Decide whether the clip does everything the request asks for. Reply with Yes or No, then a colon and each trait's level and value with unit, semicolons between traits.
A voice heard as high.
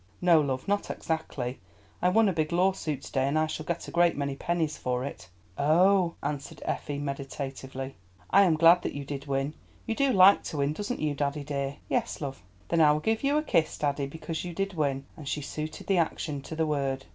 No: medium, 150 Hz